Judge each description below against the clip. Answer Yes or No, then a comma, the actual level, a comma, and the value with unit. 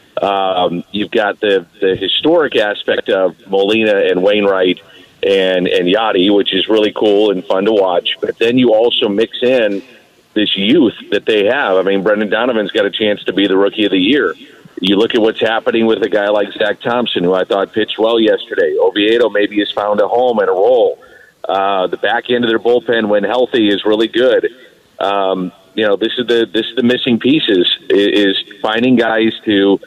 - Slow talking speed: No, average, 200 wpm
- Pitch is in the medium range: No, low, 115 Hz